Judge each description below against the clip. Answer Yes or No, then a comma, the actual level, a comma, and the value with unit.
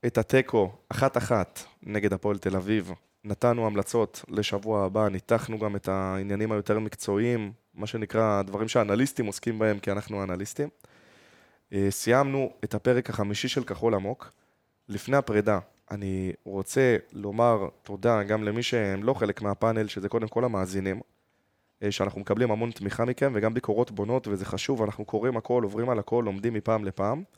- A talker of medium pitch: No, low, 105 Hz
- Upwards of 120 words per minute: Yes, fast, 150 wpm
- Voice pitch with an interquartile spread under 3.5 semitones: Yes, average, 2.8 semitones